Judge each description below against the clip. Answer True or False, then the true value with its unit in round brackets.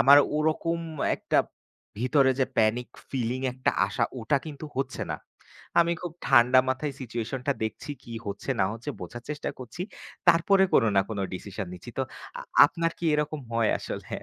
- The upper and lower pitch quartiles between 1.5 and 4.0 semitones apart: False (4.6 semitones)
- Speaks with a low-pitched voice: True (130 Hz)